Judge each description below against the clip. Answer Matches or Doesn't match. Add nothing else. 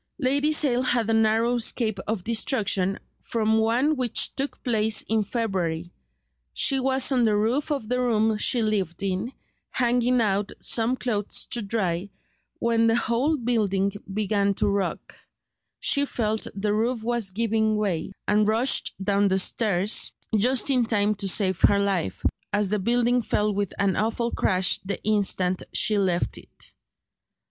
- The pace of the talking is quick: Doesn't match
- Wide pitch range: Doesn't match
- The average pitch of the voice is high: Matches